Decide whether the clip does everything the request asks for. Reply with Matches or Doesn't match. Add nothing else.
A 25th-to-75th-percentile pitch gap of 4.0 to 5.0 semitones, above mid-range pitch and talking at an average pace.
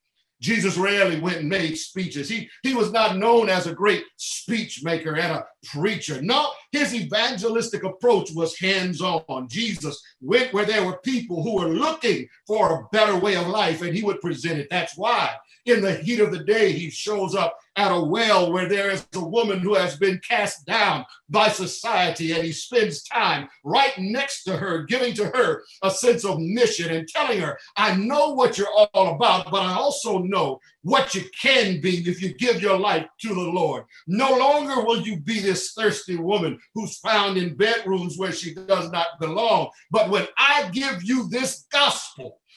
Matches